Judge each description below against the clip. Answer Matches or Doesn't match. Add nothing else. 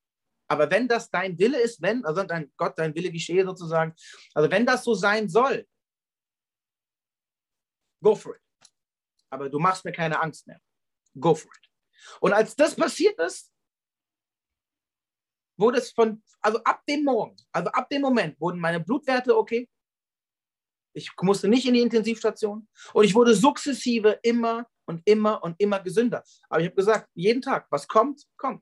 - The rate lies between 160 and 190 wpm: Matches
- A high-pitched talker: Matches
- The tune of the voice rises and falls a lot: Matches